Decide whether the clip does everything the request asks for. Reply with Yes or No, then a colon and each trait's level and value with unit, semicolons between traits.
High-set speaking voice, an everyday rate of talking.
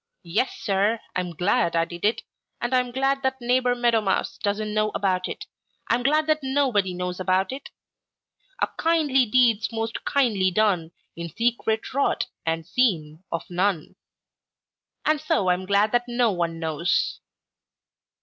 Yes: high, 215 Hz; average, 150 wpm